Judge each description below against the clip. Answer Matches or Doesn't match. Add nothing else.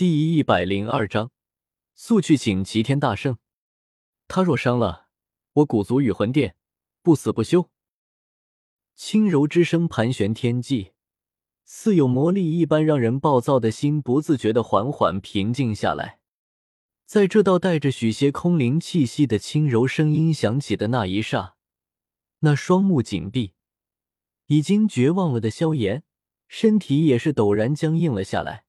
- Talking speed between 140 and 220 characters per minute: Matches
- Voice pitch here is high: Doesn't match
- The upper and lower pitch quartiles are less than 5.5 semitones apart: Doesn't match